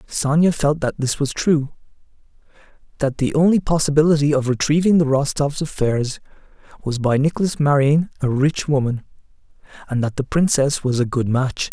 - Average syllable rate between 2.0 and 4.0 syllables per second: No, 5.2 syllables/s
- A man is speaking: Yes, male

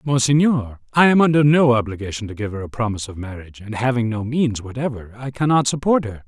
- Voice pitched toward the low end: Yes, low, 120 Hz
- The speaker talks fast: Yes, fast, 210 wpm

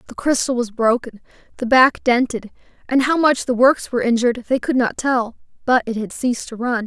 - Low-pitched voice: No, high, 245 Hz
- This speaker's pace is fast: Yes, fast, 210 wpm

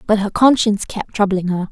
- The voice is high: Yes, high, 205 Hz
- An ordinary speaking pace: No, fast, 210 wpm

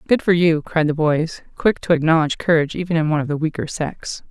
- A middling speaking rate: No, fast, 235 wpm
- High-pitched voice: No, medium, 160 Hz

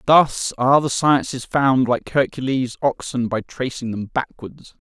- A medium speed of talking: Yes, average, 145 wpm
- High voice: No, low, 130 Hz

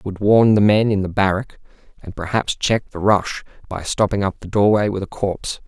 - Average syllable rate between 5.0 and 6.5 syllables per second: Yes, 5.5 syllables/s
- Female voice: No, male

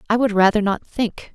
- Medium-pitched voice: No, high, 210 Hz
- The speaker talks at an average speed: No, fast, 225 wpm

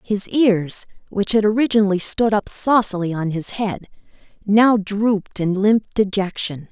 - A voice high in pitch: Yes, high, 205 Hz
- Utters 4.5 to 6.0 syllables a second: No, 4.3 syllables/s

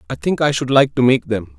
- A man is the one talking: Yes, male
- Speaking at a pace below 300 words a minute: No, fast, 305 wpm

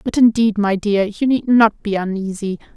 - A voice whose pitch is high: Yes, high, 210 Hz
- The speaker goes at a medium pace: Yes, average, 195 wpm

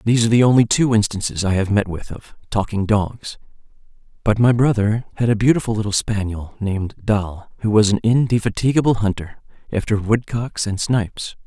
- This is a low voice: Yes, low, 110 Hz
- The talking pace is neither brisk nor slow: Yes, average, 165 wpm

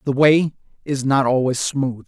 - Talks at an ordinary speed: Yes, average, 175 wpm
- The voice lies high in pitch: No, low, 135 Hz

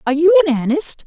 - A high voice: Yes, very high, 315 Hz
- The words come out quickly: Yes, fast, 225 wpm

